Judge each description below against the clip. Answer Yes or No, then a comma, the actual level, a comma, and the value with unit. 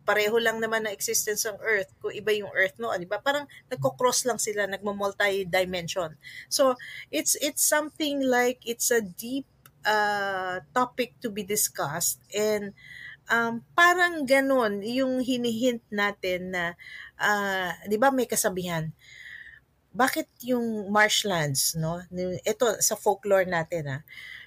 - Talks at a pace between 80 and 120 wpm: No, average, 135 wpm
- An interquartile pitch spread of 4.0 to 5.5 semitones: Yes, average, 4.8 semitones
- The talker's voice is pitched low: No, high, 210 Hz